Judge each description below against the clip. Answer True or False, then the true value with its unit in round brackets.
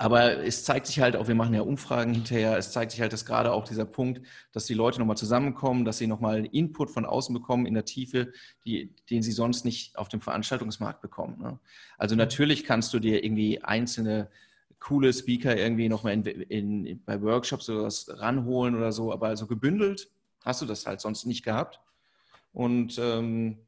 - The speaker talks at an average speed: False (200 wpm)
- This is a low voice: True (115 Hz)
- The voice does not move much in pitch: True (2.2 semitones)